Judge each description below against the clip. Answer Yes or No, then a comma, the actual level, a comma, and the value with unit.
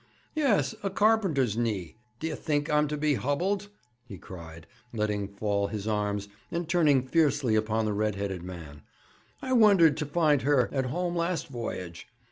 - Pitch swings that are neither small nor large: No, wide, 8.1 semitones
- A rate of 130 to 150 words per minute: No, average, 160 wpm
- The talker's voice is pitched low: Yes, low, 130 Hz